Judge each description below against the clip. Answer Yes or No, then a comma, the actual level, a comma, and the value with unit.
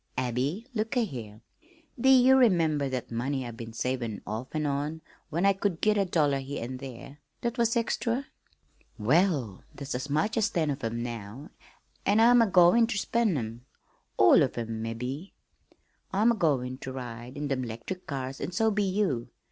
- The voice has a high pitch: No, medium, 145 Hz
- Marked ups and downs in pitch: Yes, wide, 8.3 semitones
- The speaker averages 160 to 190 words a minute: Yes, average, 180 wpm